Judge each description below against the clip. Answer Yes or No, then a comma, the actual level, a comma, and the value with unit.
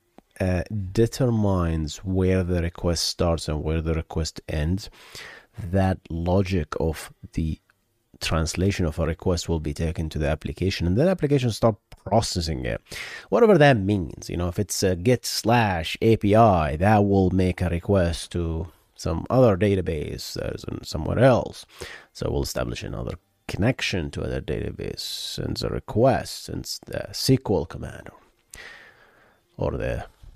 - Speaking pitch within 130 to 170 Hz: No, very low, 95 Hz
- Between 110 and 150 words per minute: Yes, average, 140 wpm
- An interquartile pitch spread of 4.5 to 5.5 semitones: Yes, average, 4.8 semitones